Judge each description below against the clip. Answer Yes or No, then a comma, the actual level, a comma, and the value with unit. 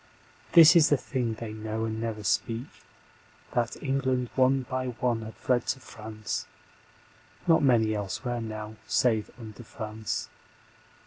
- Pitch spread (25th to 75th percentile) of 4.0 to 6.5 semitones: No, average, 2.9 semitones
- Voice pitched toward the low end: Yes, low, 115 Hz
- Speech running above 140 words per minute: No, slow, 135 wpm